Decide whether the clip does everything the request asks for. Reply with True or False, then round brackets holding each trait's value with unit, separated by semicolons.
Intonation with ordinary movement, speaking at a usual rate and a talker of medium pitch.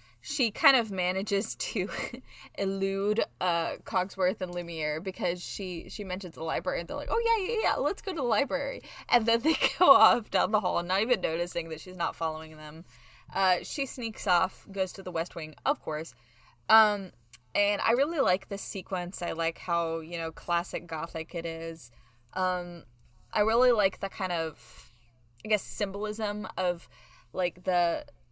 True (4.1 semitones; 180 wpm; 180 Hz)